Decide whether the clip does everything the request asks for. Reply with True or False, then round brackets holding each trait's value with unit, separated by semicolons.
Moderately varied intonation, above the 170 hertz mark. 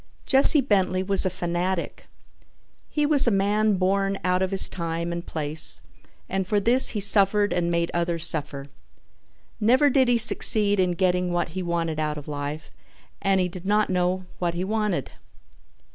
True (3.2 semitones; 185 Hz)